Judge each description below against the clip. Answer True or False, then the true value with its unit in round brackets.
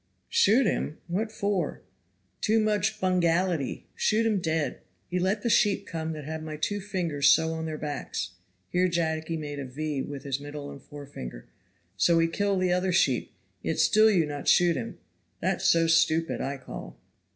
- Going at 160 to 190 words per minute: True (175 wpm)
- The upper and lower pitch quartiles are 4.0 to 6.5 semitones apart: True (4.3 semitones)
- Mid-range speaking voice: True (165 Hz)